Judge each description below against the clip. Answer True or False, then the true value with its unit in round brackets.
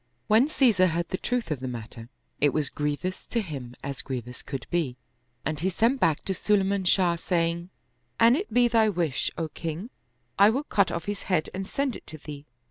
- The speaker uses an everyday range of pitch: False (6.1 semitones)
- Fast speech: True (210 wpm)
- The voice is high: False (170 Hz)